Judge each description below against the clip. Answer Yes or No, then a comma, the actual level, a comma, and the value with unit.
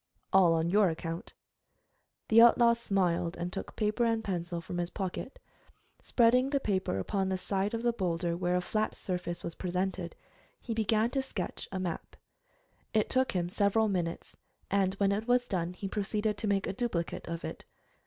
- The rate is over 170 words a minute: Yes, average, 180 wpm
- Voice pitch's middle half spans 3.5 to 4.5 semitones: Yes, average, 4.0 semitones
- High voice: Yes, high, 195 Hz